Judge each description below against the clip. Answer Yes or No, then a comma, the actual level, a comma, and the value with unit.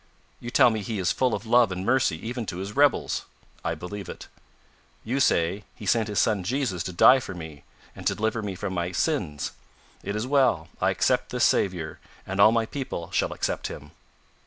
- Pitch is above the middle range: No, low, 105 Hz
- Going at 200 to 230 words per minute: Yes, fast, 205 wpm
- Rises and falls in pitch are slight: No, average, 5.1 semitones